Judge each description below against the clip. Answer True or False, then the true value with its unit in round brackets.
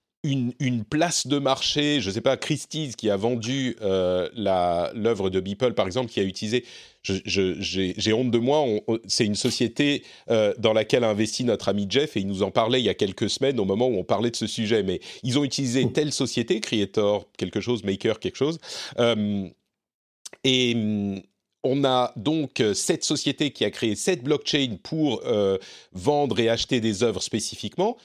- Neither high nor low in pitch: False (120 Hz)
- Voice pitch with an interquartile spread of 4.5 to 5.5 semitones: True (4.8 semitones)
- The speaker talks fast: False (200 wpm)